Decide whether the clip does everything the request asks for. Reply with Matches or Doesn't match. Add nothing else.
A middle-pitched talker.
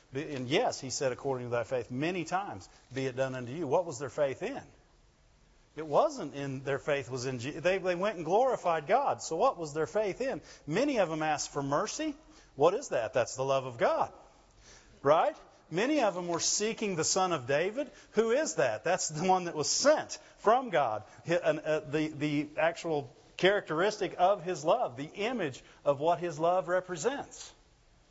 Matches